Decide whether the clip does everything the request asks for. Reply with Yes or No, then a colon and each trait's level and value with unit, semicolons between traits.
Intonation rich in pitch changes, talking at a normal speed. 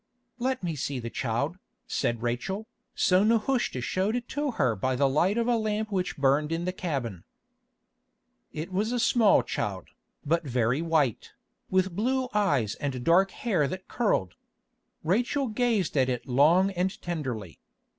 Yes: wide, 8.3 semitones; average, 155 wpm